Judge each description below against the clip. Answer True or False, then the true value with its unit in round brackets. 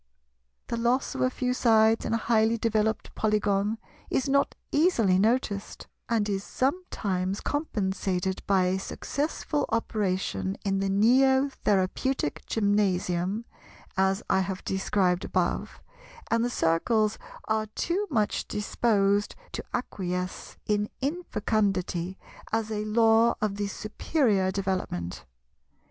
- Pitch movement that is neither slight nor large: True (3.3 semitones)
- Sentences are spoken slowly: True (120 wpm)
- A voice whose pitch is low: False (210 Hz)